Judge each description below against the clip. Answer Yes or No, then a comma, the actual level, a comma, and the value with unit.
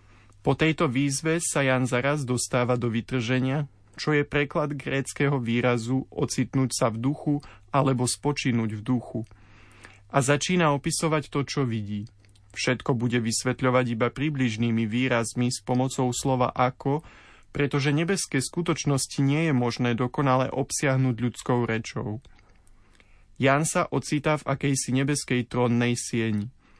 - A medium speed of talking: Yes, average, 125 wpm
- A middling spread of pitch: Yes, average, 3.3 semitones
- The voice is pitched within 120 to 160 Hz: Yes, low, 130 Hz